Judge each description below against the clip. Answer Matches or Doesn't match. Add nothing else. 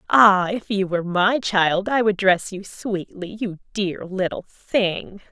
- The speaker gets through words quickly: Doesn't match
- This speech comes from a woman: Matches